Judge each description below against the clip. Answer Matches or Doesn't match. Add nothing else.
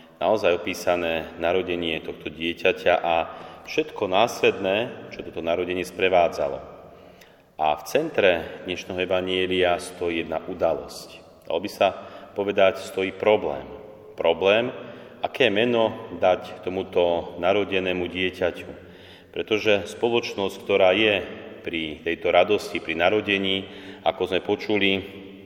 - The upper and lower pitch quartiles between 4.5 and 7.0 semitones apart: Doesn't match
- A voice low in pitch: Matches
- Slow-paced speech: Matches